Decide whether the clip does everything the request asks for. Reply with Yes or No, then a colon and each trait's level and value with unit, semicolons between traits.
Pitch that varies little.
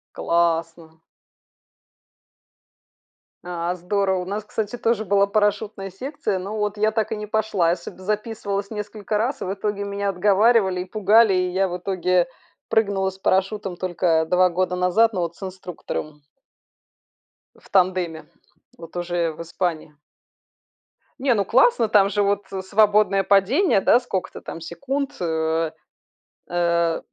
No: average, 3.0 semitones